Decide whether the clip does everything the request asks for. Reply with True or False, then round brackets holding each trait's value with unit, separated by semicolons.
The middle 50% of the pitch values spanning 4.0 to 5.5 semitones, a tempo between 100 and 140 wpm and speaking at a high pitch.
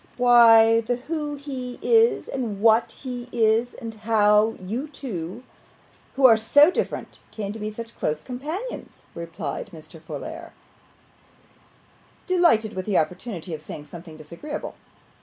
True (5.1 semitones; 135 wpm; 225 Hz)